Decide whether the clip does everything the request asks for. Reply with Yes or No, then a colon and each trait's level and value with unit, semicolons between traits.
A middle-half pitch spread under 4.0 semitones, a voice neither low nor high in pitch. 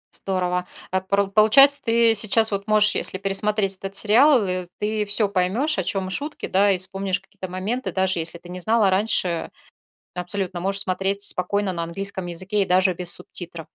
No: narrow, 2.4 semitones; high, 195 Hz